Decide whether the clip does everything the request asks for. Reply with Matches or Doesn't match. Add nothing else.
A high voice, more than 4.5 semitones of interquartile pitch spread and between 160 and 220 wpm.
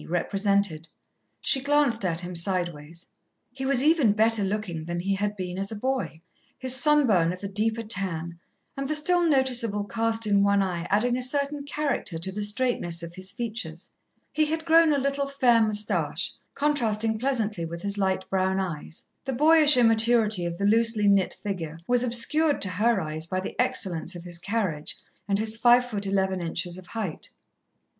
Matches